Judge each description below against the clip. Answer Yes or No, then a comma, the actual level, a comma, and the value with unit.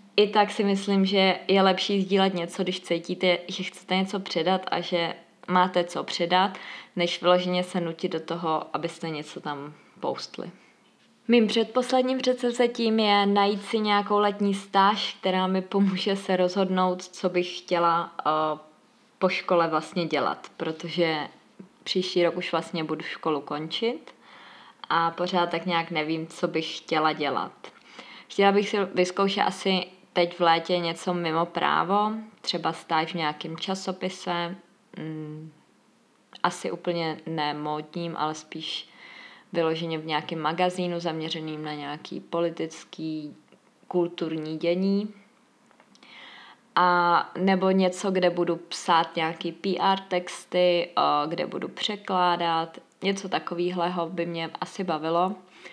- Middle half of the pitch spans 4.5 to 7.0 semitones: No, narrow, 2.6 semitones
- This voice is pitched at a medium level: Yes, medium, 180 Hz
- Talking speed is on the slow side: No, average, 130 wpm